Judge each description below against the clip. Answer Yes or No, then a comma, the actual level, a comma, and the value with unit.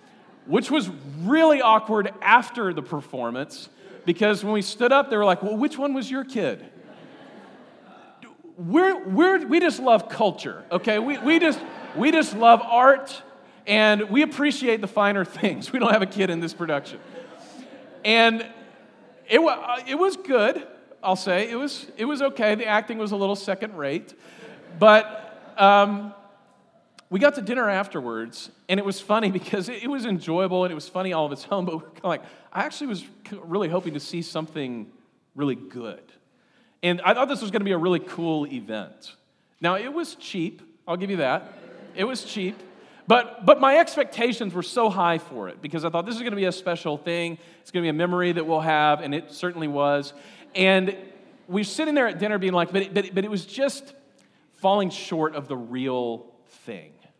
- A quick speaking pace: No, average, 190 wpm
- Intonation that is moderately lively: No, wide, 6.1 semitones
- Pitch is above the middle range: Yes, high, 200 Hz